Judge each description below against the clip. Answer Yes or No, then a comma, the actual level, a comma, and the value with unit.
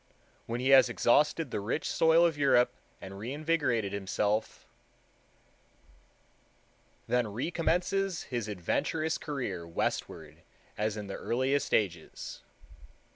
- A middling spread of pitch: No, wide, 6.8 semitones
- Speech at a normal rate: No, slow, 105 wpm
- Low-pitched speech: Yes, low, 120 Hz